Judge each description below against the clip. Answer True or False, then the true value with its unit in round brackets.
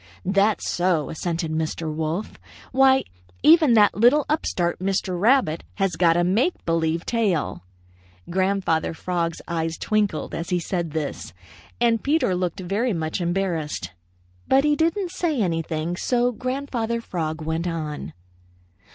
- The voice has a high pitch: False (180 Hz)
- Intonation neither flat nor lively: False (6.1 semitones)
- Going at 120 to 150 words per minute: True (135 wpm)